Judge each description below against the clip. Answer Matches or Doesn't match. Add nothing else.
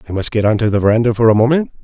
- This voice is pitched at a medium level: Doesn't match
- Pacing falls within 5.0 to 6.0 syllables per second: Doesn't match